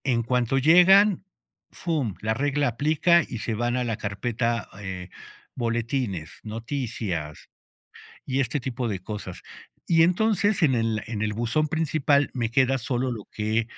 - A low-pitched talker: Yes, low, 120 Hz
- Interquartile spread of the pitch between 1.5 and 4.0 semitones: No, average, 4.7 semitones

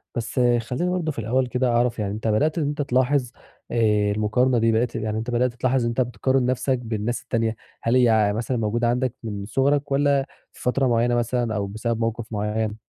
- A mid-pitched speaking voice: No, low, 120 Hz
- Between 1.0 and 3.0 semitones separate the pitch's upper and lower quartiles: Yes, narrow, 2.6 semitones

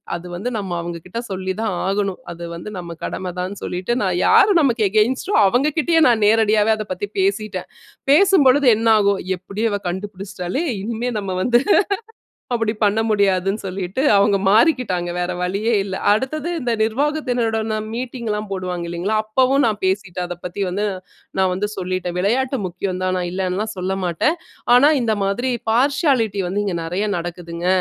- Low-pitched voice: No, high, 205 Hz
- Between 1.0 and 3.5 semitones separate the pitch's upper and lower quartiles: No, average, 4.2 semitones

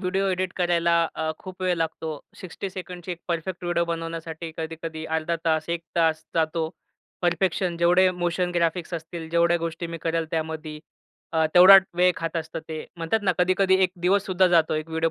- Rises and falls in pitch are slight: Yes, narrow, 1.9 semitones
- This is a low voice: No, medium, 170 Hz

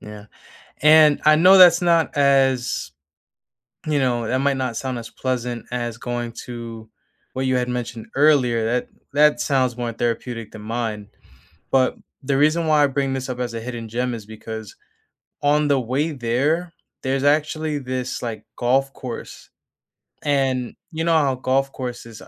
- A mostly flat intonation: No, average, 3.4 semitones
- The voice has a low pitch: Yes, low, 130 Hz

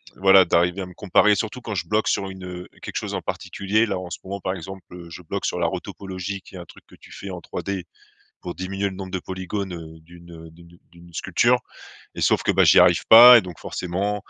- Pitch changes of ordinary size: No, narrow, 2.1 semitones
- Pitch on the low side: Yes, very low, 95 Hz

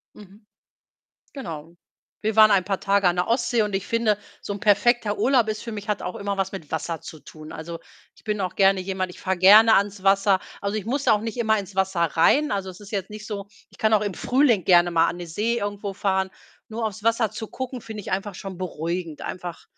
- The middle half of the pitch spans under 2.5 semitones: No, average, 2.8 semitones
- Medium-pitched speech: No, high, 200 Hz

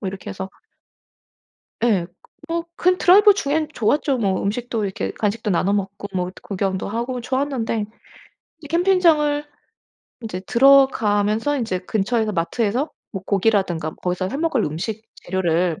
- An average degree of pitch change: No, wide, 6.4 semitones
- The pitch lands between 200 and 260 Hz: Yes, high, 220 Hz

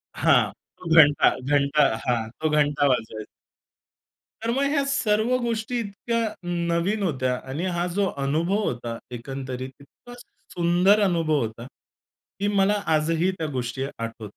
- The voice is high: No, medium, 165 Hz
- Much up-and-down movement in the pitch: Yes, wide, 7.1 semitones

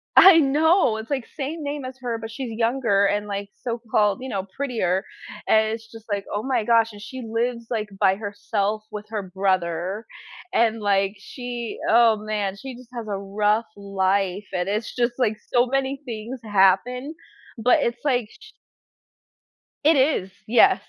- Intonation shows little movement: No, average, 3.6 semitones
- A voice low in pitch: No, high, 225 Hz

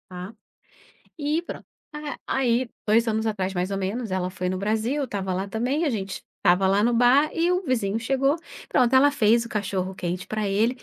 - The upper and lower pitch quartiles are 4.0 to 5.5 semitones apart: Yes, average, 5.1 semitones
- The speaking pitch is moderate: No, high, 220 Hz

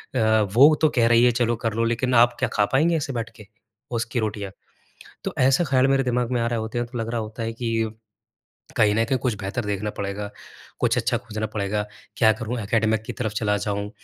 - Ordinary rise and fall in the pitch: No, narrow, 2.1 semitones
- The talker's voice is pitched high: No, low, 115 Hz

